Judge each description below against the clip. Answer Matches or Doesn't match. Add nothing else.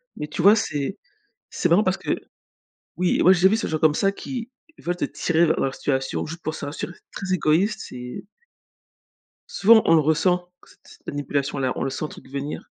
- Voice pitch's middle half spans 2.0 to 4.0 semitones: Doesn't match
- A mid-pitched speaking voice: Matches